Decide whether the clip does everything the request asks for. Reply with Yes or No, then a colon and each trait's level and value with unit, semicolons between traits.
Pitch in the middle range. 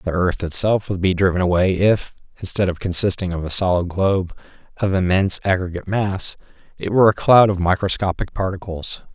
No: very low, 95 Hz